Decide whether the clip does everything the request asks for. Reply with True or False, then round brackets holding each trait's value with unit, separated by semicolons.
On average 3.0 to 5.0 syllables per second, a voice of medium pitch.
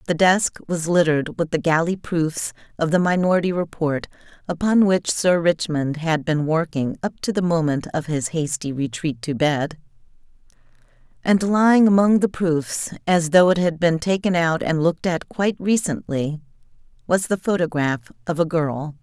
True (4.8 syllables/s; 165 Hz)